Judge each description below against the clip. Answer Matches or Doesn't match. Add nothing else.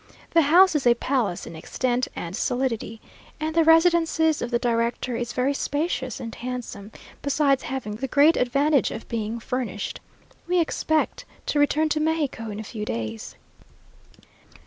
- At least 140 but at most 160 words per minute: Matches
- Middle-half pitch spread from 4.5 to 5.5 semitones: Matches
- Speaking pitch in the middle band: Doesn't match